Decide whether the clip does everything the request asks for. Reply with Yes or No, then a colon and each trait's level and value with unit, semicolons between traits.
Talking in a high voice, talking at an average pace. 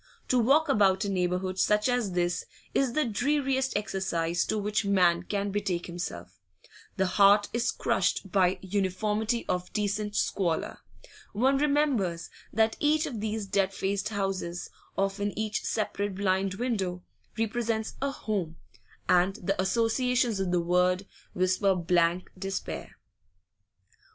No: high, 200 Hz; slow, 130 wpm